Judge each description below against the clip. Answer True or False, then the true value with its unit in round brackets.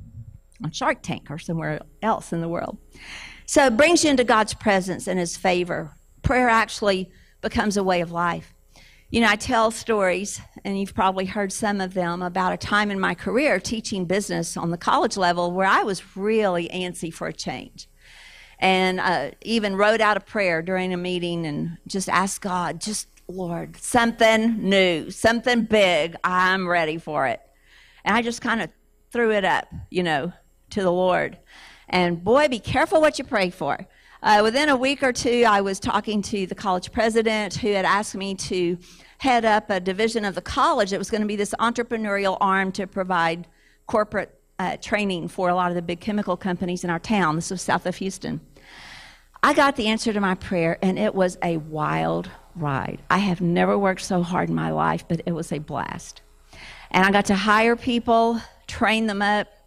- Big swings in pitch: False (3.5 semitones)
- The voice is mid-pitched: False (195 Hz)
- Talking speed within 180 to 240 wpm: True (195 wpm)